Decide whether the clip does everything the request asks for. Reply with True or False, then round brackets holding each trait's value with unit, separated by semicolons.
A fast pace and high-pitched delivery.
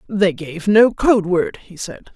False (195 wpm; 195 Hz)